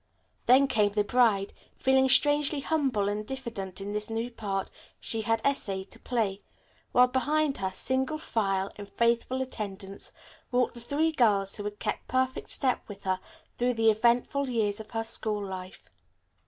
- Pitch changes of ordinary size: Yes, average, 4.3 semitones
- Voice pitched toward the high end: Yes, high, 225 Hz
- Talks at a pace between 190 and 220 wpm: No, average, 165 wpm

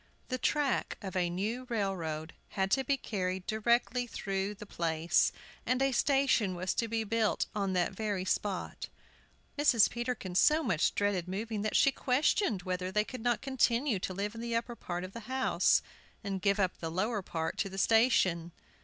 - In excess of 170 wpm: Yes, average, 180 wpm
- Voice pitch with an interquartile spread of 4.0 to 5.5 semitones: Yes, average, 4.4 semitones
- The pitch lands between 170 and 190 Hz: No, high, 210 Hz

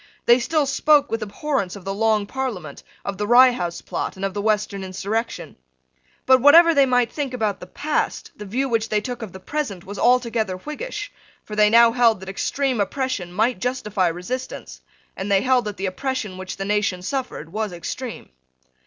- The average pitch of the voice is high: Yes, high, 220 Hz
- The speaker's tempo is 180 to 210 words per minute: Yes, average, 190 wpm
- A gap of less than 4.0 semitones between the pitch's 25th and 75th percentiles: No, average, 4.9 semitones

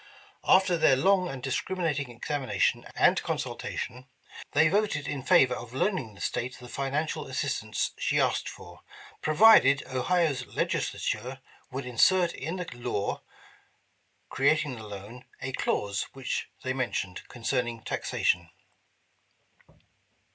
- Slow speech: Yes, slow, 120 wpm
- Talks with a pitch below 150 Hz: Yes, low, 135 Hz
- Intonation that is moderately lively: Yes, average, 4.5 semitones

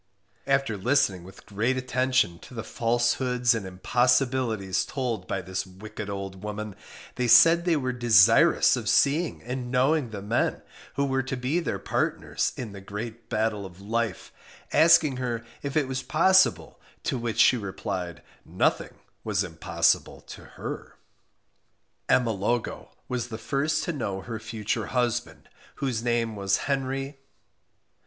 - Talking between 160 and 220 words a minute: No, average, 145 wpm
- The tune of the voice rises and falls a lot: No, average, 4.1 semitones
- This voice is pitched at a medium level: No, low, 120 Hz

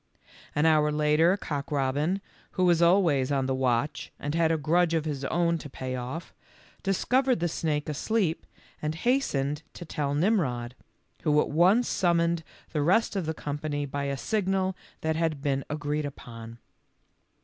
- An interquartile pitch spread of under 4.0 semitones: Yes, average, 3.4 semitones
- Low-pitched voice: No, medium, 155 Hz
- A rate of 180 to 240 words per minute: No, average, 165 wpm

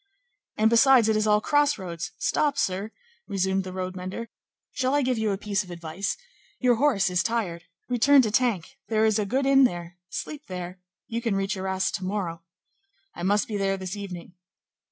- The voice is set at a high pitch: Yes, high, 205 Hz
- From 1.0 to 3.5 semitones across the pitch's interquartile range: No, average, 4.0 semitones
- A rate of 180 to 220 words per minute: Yes, average, 190 wpm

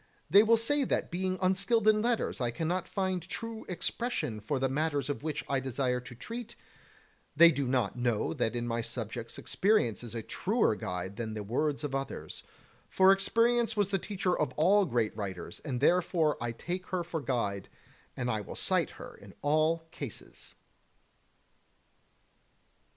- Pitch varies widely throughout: Yes, wide, 7.9 semitones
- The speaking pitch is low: No, medium, 150 Hz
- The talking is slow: No, average, 165 wpm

